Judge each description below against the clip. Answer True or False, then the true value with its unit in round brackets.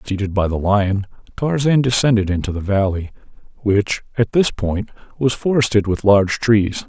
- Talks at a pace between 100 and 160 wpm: True (155 wpm)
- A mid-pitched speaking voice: False (105 Hz)